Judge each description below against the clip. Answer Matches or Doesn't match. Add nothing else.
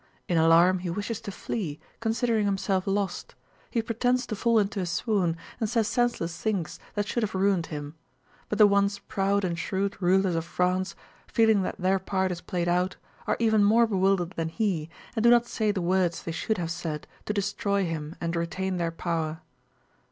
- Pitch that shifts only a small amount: Doesn't match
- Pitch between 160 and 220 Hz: Matches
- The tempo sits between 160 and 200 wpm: Matches